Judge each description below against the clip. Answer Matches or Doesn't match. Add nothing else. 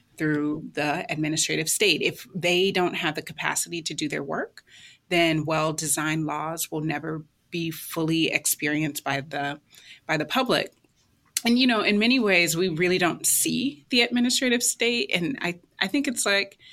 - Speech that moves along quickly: Doesn't match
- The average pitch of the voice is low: Doesn't match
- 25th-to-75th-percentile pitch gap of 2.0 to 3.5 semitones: Doesn't match